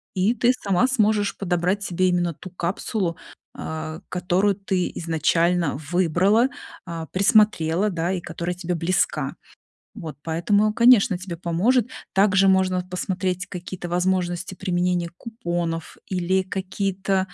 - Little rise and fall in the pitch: Yes, narrow, 2.2 semitones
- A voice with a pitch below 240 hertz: Yes, medium, 185 Hz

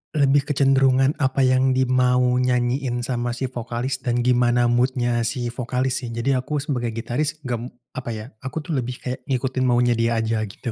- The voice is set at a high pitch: No, low, 125 Hz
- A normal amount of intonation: No, narrow, 1.6 semitones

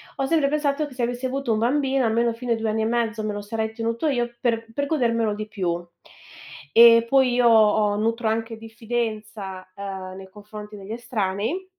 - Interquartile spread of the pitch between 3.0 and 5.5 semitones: No, narrow, 2.5 semitones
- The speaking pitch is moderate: No, high, 225 Hz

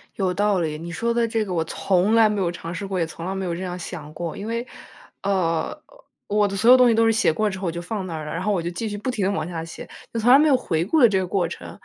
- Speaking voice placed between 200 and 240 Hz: No, high, 190 Hz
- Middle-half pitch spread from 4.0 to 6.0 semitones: Yes, average, 4.3 semitones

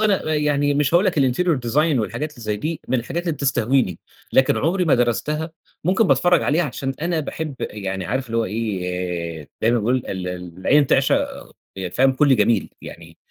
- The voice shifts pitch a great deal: Yes, wide, 6.6 semitones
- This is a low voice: Yes, low, 130 Hz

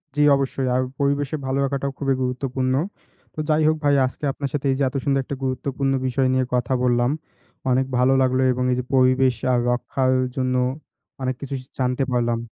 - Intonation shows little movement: Yes, narrow, 1.5 semitones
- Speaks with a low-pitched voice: Yes, low, 130 Hz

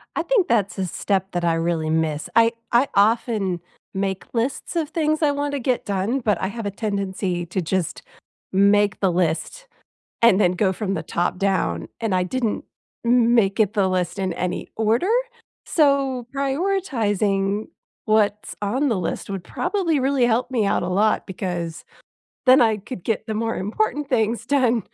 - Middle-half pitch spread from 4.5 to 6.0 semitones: Yes, average, 4.9 semitones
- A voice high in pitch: Yes, high, 210 Hz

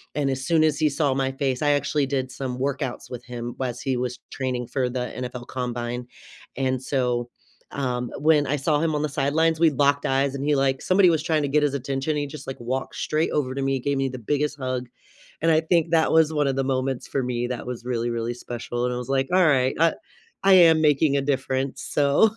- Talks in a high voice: No, low, 135 Hz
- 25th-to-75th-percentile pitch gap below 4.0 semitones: Yes, average, 2.8 semitones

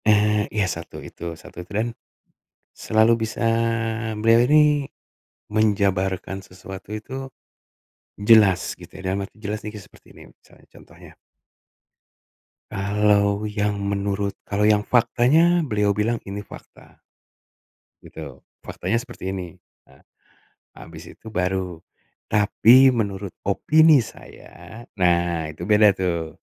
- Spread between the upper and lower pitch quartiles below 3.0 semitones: Yes, narrow, 2.5 semitones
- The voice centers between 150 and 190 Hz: No, low, 105 Hz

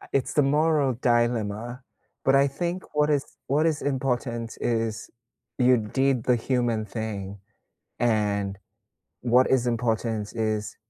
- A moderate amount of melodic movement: Yes, average, 3.5 semitones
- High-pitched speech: No, low, 120 Hz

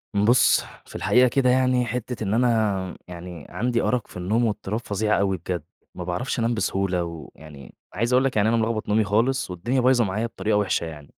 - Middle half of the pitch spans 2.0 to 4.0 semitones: No, average, 4.5 semitones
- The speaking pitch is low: Yes, low, 110 Hz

